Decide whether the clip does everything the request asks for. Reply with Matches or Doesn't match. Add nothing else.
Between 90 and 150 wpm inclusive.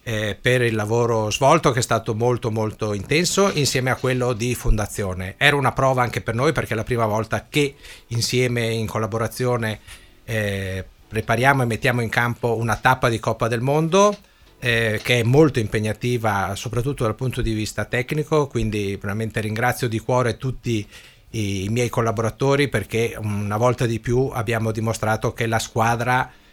Doesn't match